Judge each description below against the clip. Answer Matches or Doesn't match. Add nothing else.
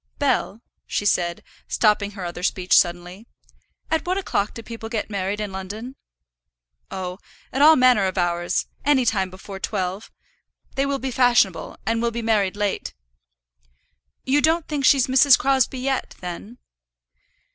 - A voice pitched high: Matches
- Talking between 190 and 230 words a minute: Doesn't match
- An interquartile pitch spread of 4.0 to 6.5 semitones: Matches